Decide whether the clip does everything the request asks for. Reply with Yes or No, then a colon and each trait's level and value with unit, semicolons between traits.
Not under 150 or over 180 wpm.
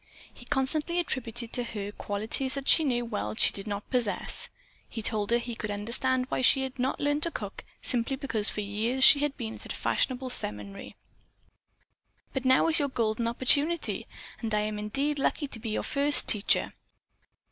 No: average, 195 wpm